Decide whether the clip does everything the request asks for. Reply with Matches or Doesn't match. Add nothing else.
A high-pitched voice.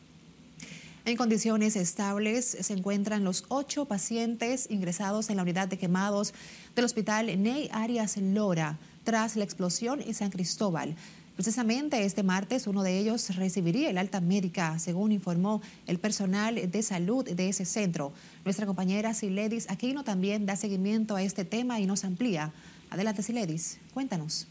Matches